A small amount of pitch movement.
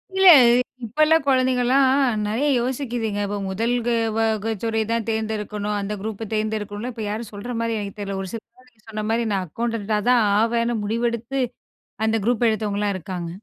Yes: narrow, 2.3 semitones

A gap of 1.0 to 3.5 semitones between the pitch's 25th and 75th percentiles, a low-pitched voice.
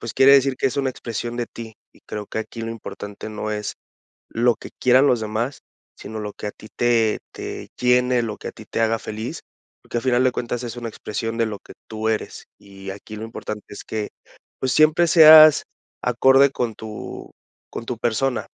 Yes: average, 2.7 semitones; low, 115 Hz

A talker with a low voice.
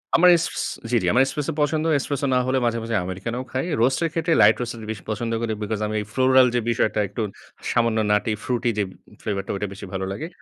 Yes: low, 120 Hz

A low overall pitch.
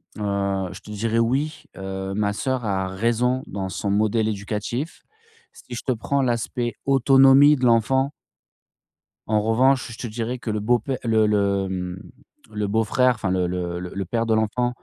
Yes: low, 110 Hz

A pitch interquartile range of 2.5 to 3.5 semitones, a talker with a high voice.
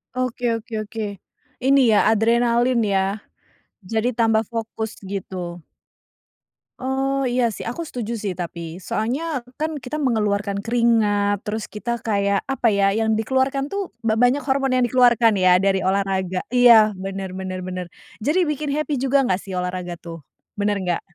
No: average, 4.3 semitones; high, 220 Hz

